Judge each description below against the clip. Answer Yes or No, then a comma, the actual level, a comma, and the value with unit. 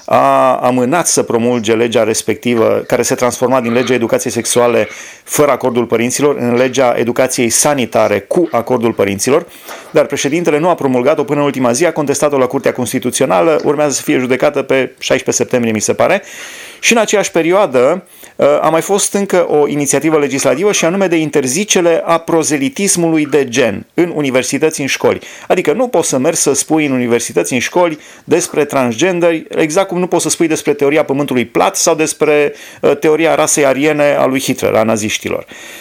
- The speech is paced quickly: Yes, fast, 175 wpm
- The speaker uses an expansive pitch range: No, average, 4.4 semitones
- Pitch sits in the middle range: Yes, medium, 145 Hz